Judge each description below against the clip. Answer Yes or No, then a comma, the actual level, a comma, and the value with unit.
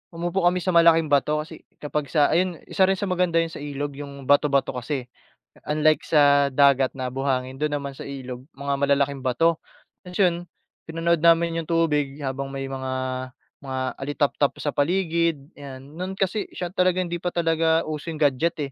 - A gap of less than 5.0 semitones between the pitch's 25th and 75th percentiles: Yes, average, 3.2 semitones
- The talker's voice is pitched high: No, medium, 150 Hz